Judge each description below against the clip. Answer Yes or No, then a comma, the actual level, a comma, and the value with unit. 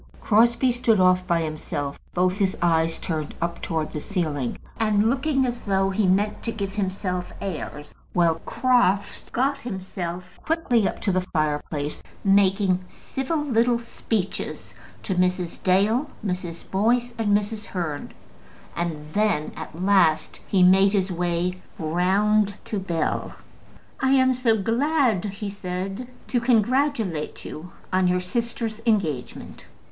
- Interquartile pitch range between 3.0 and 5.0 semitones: Yes, average, 4.3 semitones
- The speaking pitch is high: Yes, high, 195 Hz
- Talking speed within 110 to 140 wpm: Yes, slow, 135 wpm